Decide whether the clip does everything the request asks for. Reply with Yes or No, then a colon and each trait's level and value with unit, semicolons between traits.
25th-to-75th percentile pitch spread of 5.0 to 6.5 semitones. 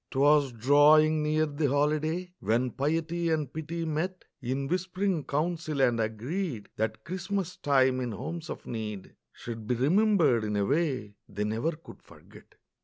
Yes: wide, 5.4 semitones